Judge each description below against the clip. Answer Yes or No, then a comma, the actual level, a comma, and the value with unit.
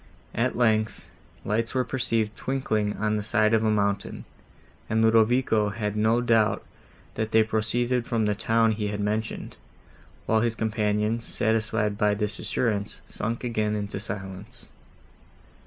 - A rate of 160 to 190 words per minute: No, average, 140 wpm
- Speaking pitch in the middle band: No, low, 110 Hz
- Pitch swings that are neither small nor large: No, narrow, 1.5 semitones